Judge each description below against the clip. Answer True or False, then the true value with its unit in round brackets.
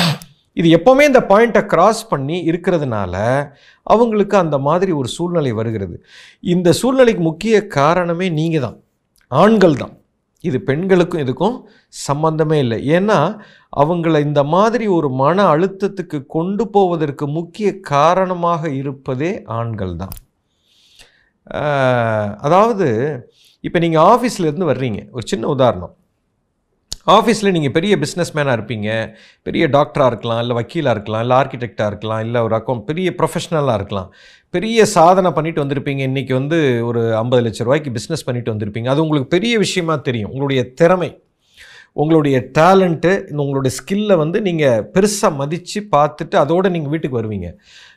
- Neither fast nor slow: False (130 wpm)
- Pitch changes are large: True (6.1 semitones)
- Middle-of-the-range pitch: True (160 Hz)